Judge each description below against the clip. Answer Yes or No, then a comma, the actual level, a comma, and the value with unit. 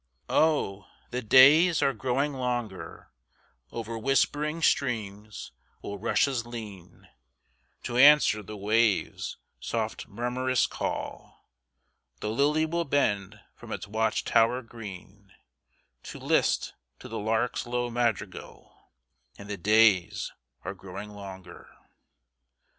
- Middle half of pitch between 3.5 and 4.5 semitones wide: Yes, average, 4.0 semitones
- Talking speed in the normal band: No, slow, 110 wpm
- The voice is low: Yes, low, 115 Hz